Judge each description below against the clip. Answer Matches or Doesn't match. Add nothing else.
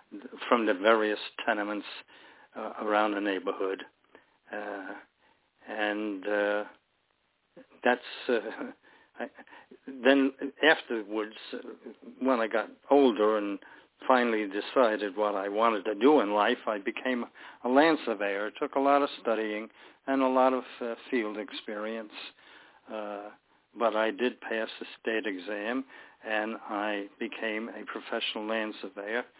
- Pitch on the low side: Matches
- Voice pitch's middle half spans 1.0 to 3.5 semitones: Matches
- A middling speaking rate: Doesn't match